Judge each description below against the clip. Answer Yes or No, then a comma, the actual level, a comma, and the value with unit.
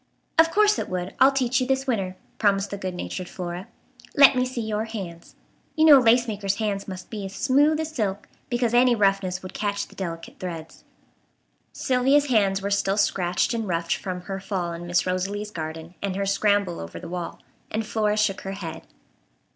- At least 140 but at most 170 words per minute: No, average, 195 wpm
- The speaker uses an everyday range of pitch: Yes, average, 4.4 semitones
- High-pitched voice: Yes, high, 200 Hz